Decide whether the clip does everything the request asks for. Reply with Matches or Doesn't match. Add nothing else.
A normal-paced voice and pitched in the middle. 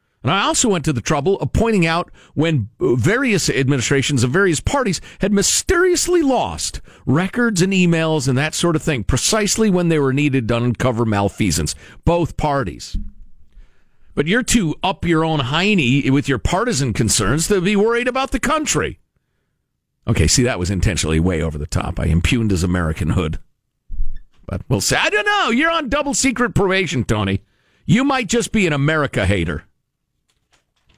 Matches